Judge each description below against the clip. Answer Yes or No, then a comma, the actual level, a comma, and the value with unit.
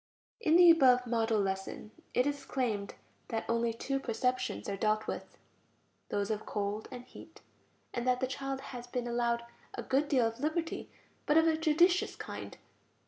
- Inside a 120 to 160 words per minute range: No, average, 170 wpm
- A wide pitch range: No, average, 3.6 semitones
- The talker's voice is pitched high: Yes, very high, 250 Hz